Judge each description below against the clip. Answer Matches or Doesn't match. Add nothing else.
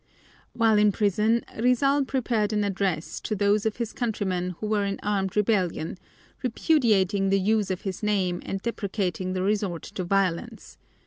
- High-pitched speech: Matches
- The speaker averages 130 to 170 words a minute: Matches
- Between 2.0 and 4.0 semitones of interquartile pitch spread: Matches